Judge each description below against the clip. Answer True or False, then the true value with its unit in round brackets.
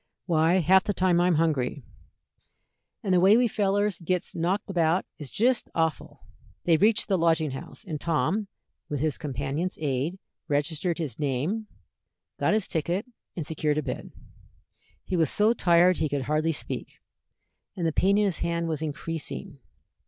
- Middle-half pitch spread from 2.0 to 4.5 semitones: True (3.7 semitones)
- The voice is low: False (170 Hz)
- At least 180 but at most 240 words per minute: False (160 wpm)